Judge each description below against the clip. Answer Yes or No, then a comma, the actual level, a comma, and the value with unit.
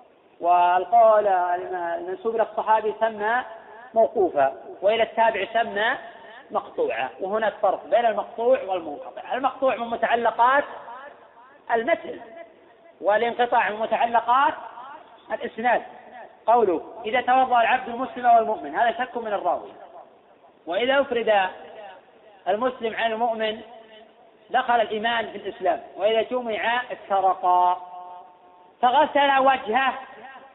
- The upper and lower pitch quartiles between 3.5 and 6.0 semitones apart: No, average, 3.1 semitones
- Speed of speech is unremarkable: Yes, average, 90 wpm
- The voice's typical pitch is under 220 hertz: No, high, 230 Hz